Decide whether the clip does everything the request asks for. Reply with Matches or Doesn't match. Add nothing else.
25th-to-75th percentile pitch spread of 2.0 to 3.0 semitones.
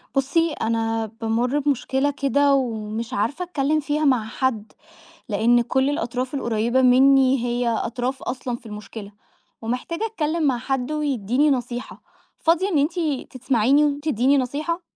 Doesn't match